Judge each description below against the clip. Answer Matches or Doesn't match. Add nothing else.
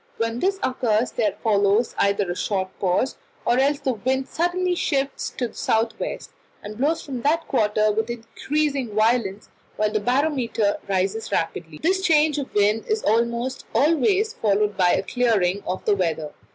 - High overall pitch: Matches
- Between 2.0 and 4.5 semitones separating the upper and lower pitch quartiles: Doesn't match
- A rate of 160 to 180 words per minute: Matches